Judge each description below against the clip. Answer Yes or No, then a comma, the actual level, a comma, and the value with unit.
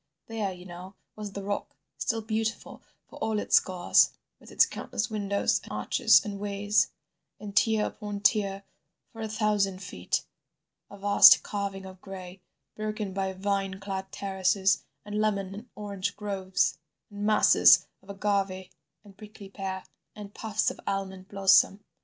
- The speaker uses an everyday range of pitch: No, narrow, 1.6 semitones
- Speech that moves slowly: No, average, 145 wpm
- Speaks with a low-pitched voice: No, high, 200 Hz